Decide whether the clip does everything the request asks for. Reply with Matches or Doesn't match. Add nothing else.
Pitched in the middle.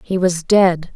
Matches